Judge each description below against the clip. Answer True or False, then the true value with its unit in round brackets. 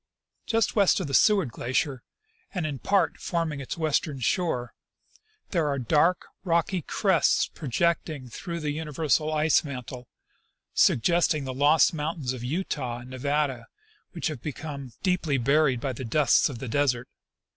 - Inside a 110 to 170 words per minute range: True (155 wpm)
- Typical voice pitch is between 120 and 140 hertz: False (150 Hz)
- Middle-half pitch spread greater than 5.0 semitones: False (4.3 semitones)